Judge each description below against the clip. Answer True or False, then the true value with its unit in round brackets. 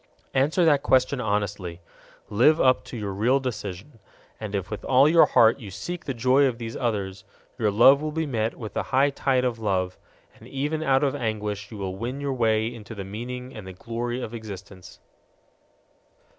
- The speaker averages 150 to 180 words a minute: False (190 wpm)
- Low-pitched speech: True (115 Hz)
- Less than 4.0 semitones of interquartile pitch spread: False (4.4 semitones)